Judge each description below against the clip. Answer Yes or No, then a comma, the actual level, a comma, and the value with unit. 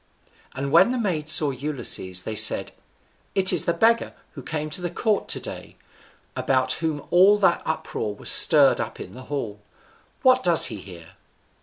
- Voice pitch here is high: No, medium, 155 Hz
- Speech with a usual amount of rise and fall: No, wide, 6.0 semitones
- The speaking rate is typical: Yes, average, 175 wpm